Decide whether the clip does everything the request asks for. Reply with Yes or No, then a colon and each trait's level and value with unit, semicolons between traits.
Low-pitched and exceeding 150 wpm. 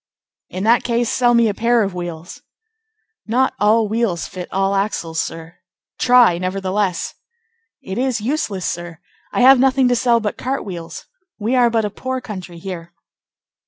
No: high, 210 Hz; average, 160 wpm